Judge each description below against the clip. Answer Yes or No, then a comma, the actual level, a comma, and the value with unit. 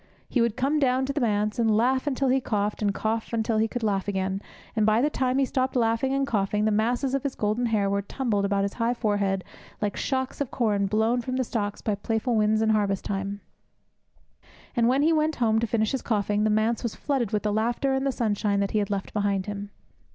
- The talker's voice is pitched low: No, high, 220 Hz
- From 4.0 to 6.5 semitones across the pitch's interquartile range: No, average, 3.6 semitones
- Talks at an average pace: No, fast, 240 wpm